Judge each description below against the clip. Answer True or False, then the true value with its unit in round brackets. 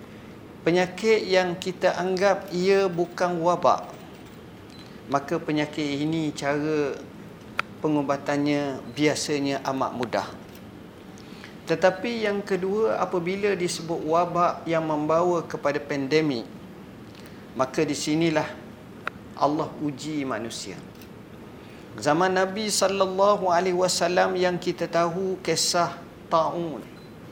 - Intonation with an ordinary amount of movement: True (3.7 semitones)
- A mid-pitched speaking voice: True (170 Hz)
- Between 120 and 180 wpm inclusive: False (90 wpm)